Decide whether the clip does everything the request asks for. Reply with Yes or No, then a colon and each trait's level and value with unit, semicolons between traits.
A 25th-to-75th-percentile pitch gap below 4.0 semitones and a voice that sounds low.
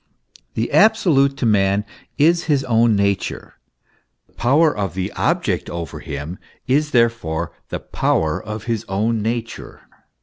No: wide, 5.6 semitones; low, 115 Hz